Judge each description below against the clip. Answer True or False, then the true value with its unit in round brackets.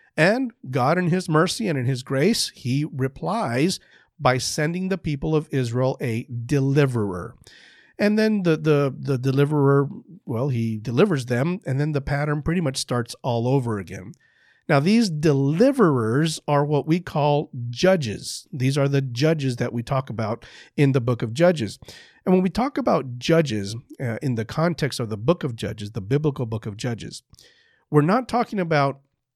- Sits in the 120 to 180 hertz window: True (140 Hz)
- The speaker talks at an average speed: True (170 wpm)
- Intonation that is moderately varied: True (4.7 semitones)